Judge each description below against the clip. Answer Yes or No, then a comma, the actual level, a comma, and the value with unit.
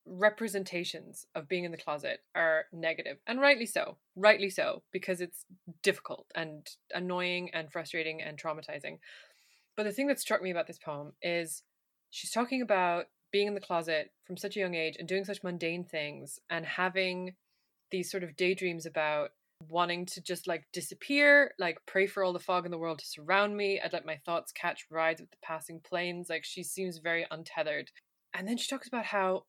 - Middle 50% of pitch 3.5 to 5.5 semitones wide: No, average, 3.1 semitones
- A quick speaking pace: No, average, 190 wpm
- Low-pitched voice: No, medium, 180 Hz